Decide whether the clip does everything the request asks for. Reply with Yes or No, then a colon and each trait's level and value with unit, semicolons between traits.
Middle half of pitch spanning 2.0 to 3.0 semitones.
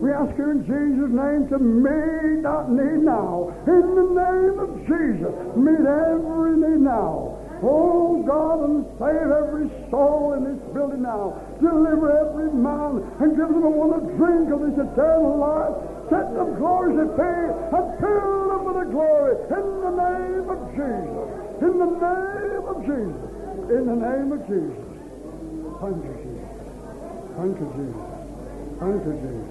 No: average, 3.6 semitones